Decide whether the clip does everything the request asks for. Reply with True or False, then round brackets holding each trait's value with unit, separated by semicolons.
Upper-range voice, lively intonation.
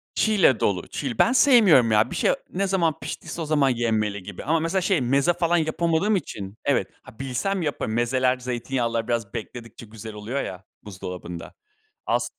False (130 Hz; 7.1 semitones)